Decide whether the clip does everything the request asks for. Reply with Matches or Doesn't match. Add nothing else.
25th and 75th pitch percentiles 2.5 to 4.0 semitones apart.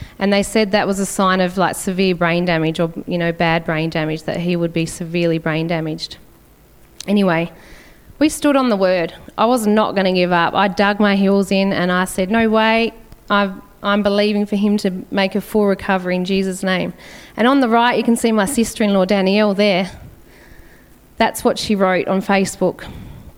Matches